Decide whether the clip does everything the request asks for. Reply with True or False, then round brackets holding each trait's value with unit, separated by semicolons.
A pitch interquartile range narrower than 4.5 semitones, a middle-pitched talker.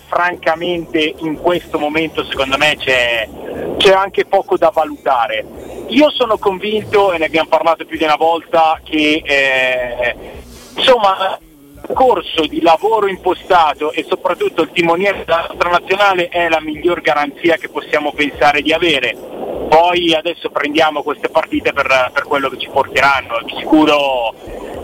True (3.5 semitones; 160 Hz)